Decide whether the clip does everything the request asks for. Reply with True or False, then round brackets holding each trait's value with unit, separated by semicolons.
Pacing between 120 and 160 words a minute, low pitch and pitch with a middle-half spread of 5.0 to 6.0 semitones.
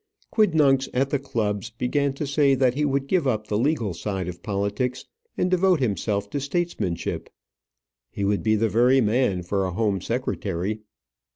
False (170 wpm; 120 Hz; 5.3 semitones)